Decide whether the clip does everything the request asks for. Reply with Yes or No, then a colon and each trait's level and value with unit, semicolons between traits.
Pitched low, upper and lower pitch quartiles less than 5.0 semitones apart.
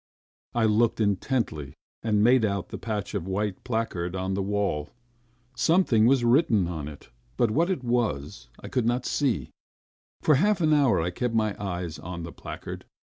No: low, 110 Hz; average, 5.3 semitones